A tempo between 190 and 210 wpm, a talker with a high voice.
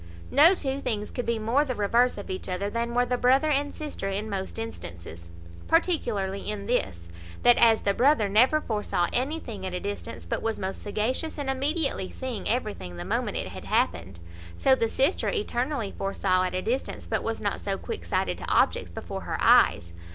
Yes: average, 195 wpm; high, 225 Hz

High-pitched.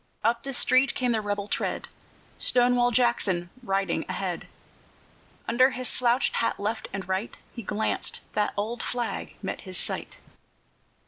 Yes: high, 235 Hz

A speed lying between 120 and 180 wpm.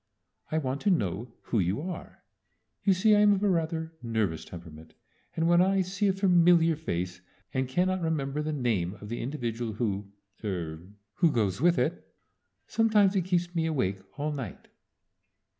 Yes: average, 165 wpm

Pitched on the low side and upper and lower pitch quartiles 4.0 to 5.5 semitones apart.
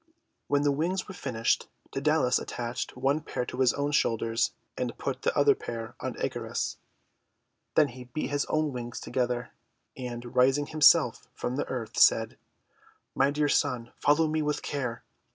No: low, 130 Hz; average, 3.4 semitones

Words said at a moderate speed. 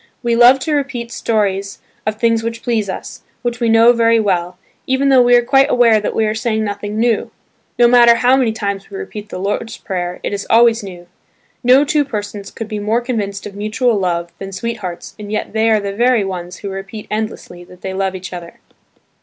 No: fast, 210 wpm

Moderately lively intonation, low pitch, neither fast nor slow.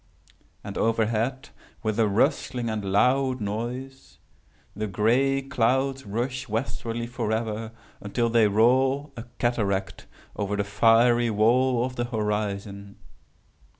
No: average, 3.2 semitones; low, 115 Hz; slow, 115 wpm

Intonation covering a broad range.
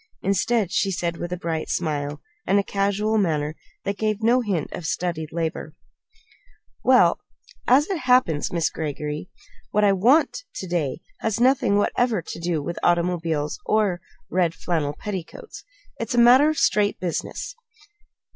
No: average, 4.9 semitones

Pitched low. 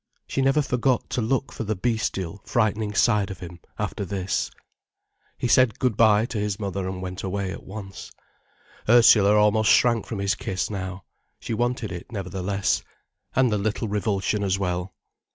Yes: low, 105 Hz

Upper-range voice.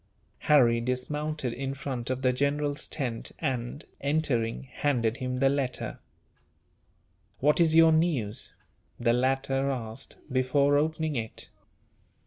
No: low, 135 Hz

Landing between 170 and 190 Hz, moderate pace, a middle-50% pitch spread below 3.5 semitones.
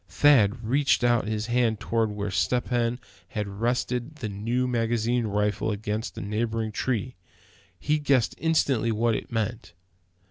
No: low, 115 Hz; average, 145 wpm; narrow, 2.6 semitones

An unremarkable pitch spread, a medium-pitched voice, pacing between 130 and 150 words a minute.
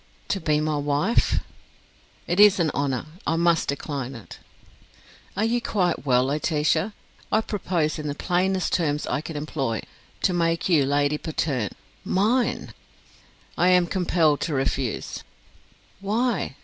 Yes: average, 4.3 semitones; medium, 160 Hz; slow, 135 wpm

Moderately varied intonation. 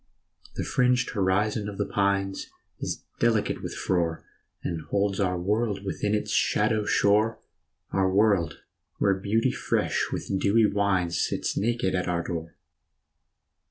No: narrow, 2.2 semitones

